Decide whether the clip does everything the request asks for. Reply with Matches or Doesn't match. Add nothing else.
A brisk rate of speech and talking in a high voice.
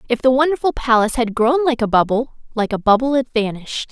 Matches